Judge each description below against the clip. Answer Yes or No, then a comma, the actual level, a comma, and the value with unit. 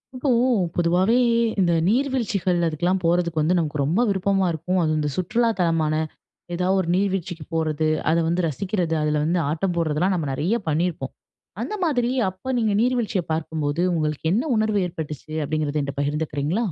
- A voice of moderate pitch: Yes, medium, 170 Hz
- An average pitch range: Yes, average, 3.9 semitones